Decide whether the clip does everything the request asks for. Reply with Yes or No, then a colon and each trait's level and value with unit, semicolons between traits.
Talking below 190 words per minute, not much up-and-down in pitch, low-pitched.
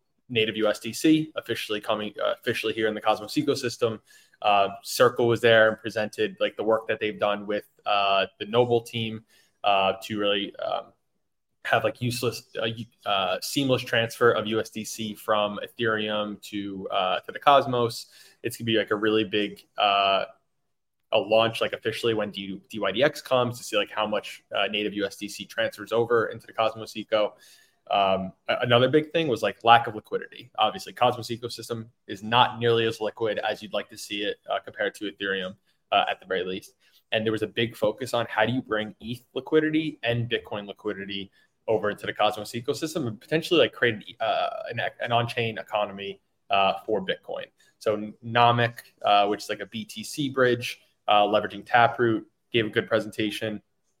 Yes: average, 180 wpm; narrow, 2.3 semitones; low, 110 Hz